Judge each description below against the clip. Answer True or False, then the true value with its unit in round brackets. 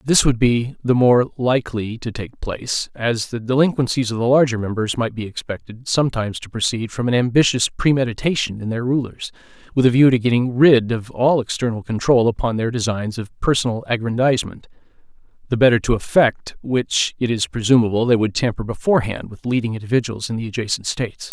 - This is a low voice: True (120 Hz)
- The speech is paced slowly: False (180 wpm)